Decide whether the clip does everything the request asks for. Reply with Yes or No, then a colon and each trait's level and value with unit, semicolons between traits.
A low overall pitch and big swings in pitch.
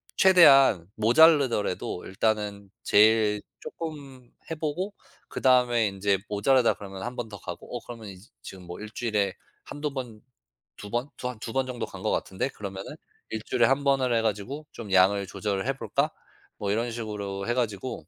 No: low, 115 Hz; average, 4.4 semitones